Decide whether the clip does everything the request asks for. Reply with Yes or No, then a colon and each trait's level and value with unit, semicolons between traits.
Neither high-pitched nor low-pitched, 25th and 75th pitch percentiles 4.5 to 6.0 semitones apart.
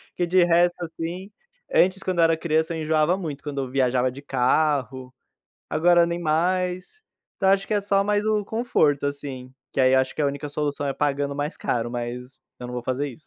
Yes: medium, 150 Hz; average, 4.9 semitones